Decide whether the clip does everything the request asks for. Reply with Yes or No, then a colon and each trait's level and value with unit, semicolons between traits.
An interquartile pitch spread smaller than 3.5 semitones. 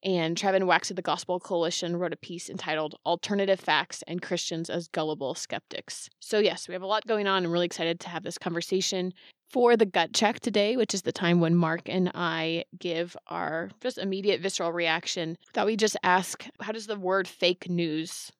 Yes: narrow, 2.6 semitones